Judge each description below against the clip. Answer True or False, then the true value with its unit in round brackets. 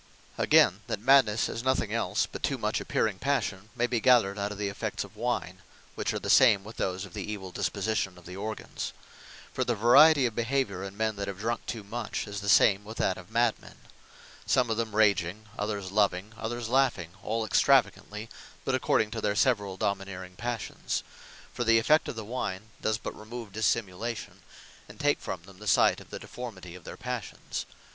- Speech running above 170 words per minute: True (200 wpm)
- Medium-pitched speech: False (110 Hz)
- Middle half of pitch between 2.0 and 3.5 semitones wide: True (3.1 semitones)